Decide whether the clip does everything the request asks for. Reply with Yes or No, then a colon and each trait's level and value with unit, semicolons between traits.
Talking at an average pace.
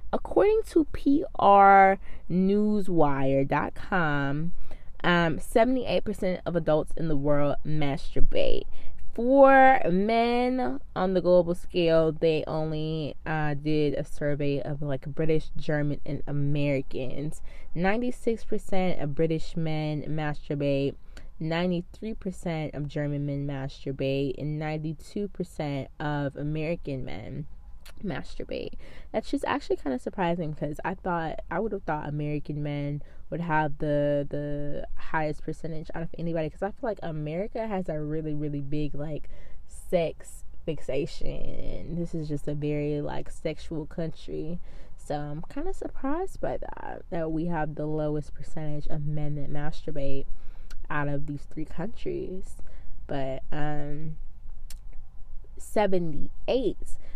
No: slow, 120 wpm